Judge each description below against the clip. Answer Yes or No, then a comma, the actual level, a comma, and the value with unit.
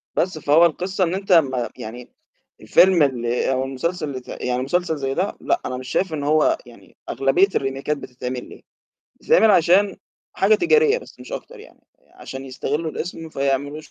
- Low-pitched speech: No, medium, 150 Hz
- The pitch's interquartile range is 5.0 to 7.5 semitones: Yes, wide, 5.5 semitones